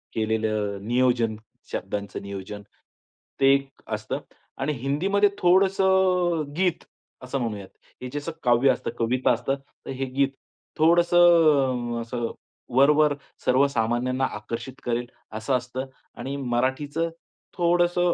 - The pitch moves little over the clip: No, wide, 5.4 semitones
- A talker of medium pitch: No, low, 130 Hz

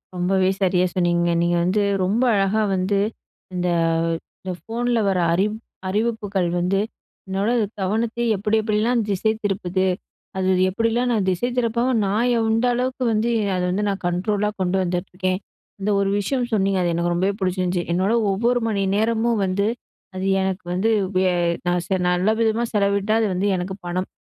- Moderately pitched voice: No, high, 195 Hz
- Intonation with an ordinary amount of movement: Yes, average, 3.2 semitones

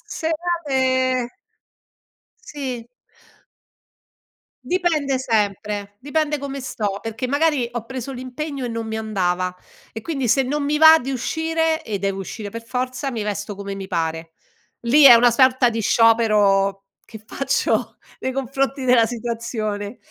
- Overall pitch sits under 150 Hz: No, high, 245 Hz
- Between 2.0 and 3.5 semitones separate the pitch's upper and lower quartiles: No, average, 4.5 semitones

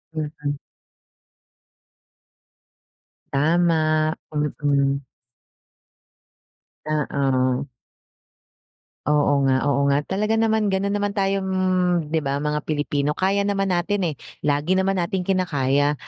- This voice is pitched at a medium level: Yes, medium, 155 Hz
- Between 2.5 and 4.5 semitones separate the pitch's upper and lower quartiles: No, average, 4.9 semitones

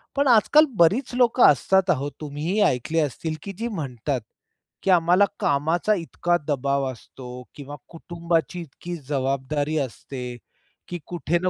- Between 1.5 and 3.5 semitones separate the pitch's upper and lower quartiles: No, average, 4.6 semitones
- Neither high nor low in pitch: Yes, medium, 160 Hz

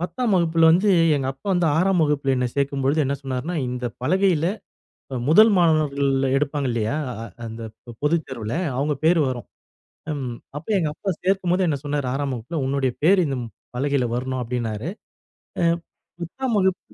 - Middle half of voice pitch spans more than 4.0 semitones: Yes, average, 4.7 semitones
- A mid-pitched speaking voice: Yes, medium, 145 Hz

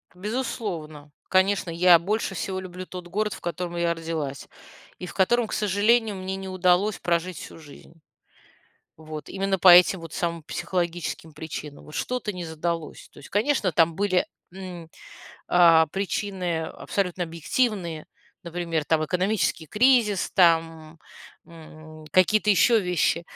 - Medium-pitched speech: Yes, medium, 180 Hz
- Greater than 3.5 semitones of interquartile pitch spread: No, average, 3.1 semitones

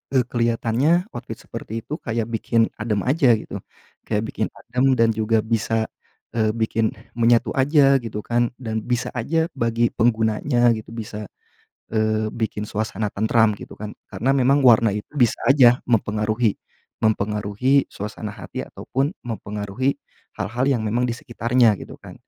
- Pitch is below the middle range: Yes, low, 115 Hz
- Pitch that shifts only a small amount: Yes, narrow, 2.3 semitones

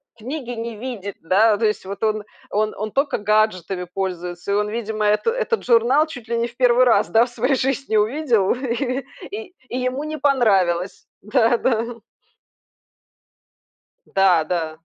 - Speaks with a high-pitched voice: Yes, high, 225 Hz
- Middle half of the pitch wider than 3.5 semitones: Yes, average, 3.9 semitones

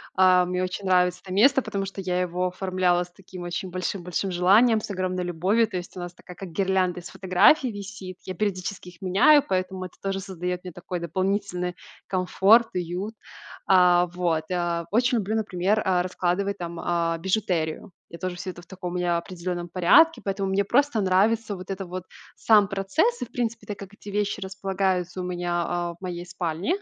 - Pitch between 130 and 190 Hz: Yes, medium, 185 Hz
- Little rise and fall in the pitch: Yes, narrow, 1.9 semitones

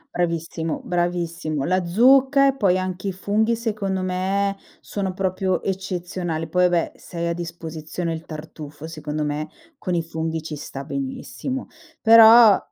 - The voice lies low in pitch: No, medium, 180 Hz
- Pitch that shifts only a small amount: No, average, 3.4 semitones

